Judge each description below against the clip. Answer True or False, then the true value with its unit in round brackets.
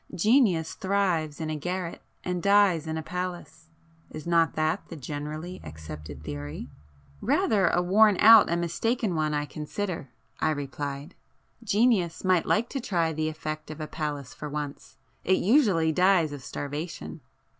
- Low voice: False (165 Hz)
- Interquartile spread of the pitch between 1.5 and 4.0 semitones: True (3.7 semitones)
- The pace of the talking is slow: False (145 wpm)